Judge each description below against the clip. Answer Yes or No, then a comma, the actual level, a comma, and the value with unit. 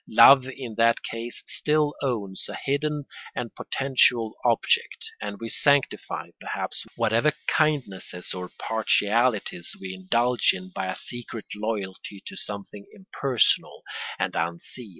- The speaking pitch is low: Yes, low, 115 Hz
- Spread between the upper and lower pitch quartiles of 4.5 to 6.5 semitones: Yes, average, 4.9 semitones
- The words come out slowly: Yes, slow, 125 wpm